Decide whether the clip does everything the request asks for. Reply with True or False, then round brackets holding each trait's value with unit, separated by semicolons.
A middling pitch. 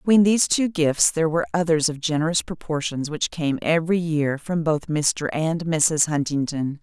True (160 Hz)